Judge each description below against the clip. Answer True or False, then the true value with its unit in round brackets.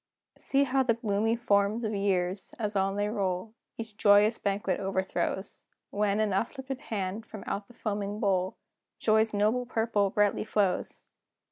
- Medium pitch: False (210 Hz)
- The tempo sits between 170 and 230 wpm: False (150 wpm)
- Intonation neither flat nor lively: False (2.1 semitones)